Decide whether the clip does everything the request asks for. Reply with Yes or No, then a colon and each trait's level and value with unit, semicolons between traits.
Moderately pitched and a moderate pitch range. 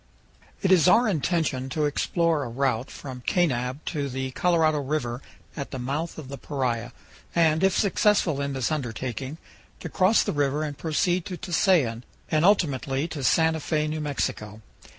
Yes: medium, 150 Hz; average, 4.1 semitones